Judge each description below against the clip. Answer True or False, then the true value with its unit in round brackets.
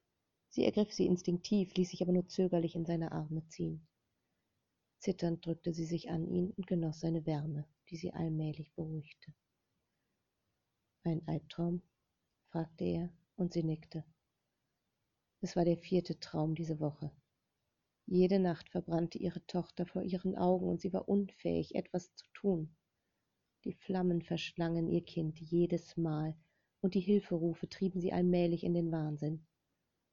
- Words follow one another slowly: False (145 wpm)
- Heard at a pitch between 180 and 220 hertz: False (170 Hz)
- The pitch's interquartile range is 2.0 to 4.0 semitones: True (2.4 semitones)